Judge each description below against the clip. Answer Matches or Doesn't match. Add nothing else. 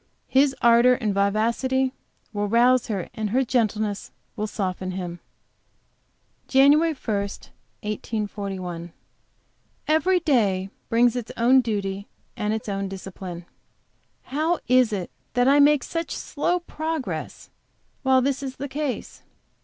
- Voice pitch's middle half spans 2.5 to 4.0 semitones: Doesn't match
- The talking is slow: Matches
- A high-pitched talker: Matches